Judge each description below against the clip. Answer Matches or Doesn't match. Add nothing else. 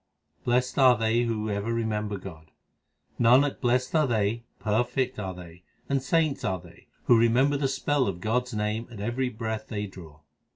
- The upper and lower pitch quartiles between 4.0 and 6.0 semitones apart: Doesn't match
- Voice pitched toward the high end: Doesn't match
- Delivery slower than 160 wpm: Doesn't match